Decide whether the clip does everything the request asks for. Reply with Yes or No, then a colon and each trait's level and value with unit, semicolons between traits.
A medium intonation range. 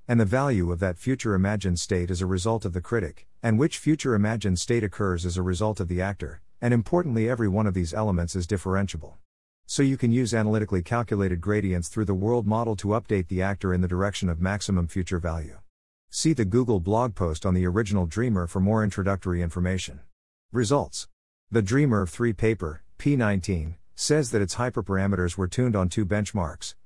Yes: average, 3.9 semitones